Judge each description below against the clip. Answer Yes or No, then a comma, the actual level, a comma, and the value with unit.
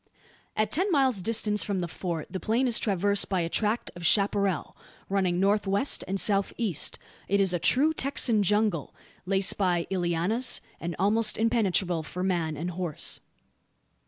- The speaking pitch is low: No, high, 195 Hz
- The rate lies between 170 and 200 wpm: No, average, 160 wpm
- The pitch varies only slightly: No, average, 3.6 semitones